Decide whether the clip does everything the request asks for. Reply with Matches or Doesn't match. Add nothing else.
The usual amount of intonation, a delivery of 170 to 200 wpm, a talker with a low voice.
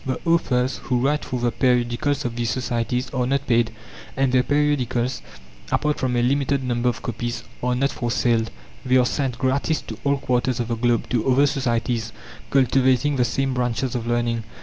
Doesn't match